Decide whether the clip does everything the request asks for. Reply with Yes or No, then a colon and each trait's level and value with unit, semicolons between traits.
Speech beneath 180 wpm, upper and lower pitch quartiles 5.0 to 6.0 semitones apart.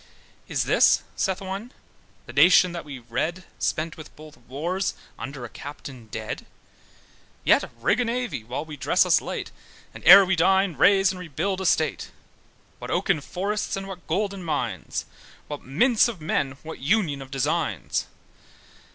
Yes: average, 160 wpm; wide, 5.4 semitones